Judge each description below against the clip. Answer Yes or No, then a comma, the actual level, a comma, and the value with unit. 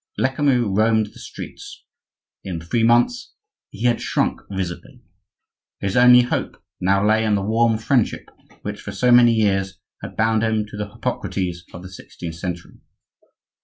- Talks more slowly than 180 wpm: Yes, average, 155 wpm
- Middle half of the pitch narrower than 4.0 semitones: Yes, average, 3.5 semitones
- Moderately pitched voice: No, low, 110 Hz